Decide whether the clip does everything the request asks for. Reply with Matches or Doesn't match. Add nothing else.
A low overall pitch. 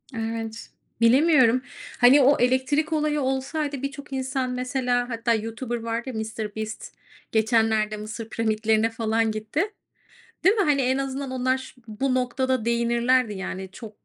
Doesn't match